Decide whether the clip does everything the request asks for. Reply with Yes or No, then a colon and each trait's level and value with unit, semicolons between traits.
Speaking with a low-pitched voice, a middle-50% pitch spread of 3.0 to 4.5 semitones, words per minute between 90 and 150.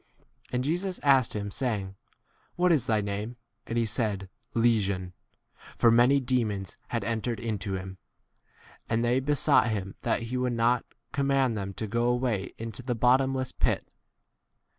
No: low, 115 Hz; average, 3.6 semitones; average, 165 wpm